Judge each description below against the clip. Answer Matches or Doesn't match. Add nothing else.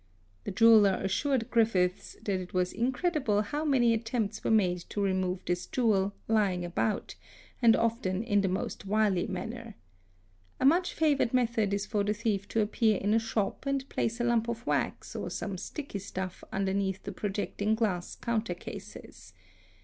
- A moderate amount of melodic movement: Matches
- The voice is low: Doesn't match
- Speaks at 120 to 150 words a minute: Doesn't match